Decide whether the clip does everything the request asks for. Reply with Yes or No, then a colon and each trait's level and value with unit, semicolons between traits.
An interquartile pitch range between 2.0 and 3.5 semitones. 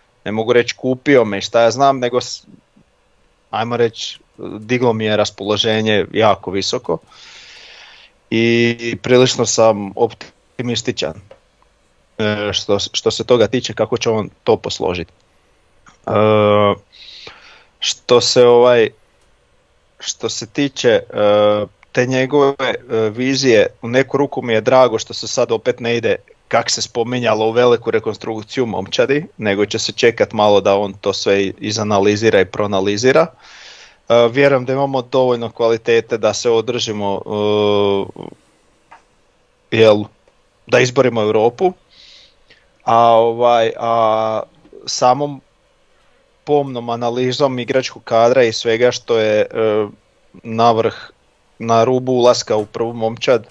Yes: average, 2.8 semitones